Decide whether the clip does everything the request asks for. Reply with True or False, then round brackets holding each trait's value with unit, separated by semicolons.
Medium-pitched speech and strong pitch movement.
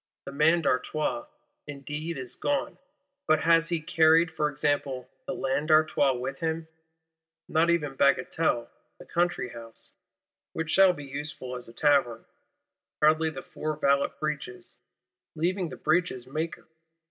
False (155 Hz; 3.0 semitones)